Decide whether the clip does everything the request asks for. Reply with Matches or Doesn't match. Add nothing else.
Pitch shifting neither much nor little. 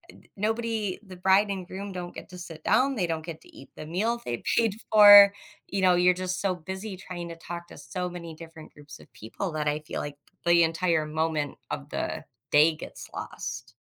Matches